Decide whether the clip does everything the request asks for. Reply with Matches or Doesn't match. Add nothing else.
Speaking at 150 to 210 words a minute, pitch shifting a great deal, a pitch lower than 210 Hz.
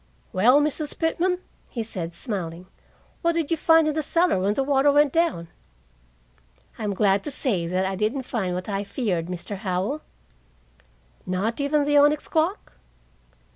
Doesn't match